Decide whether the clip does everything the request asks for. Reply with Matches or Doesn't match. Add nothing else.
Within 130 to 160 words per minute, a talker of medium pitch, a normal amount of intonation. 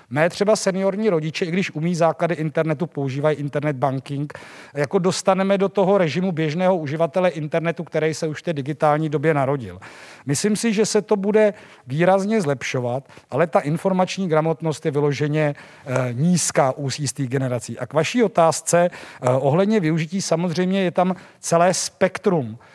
Matches